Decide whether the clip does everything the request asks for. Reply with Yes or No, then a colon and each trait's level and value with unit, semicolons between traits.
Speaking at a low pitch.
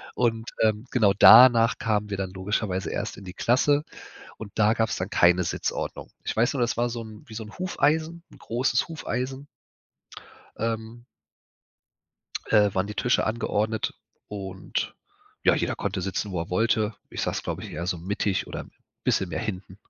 Yes: low, 110 Hz